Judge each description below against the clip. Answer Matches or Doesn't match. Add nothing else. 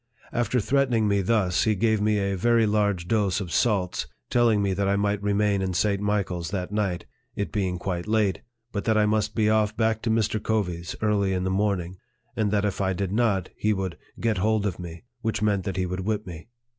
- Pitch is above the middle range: Doesn't match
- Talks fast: Matches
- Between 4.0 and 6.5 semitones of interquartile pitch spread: Doesn't match